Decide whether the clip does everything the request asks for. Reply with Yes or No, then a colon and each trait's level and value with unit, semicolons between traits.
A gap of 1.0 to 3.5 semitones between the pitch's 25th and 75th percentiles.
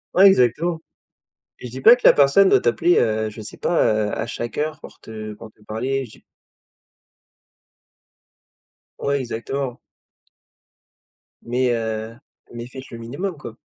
No: average, 4.0 semitones